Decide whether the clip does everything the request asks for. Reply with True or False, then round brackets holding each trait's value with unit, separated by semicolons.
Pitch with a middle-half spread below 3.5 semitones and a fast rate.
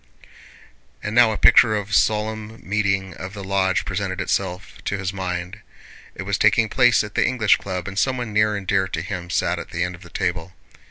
True (2.4 semitones; 210 wpm)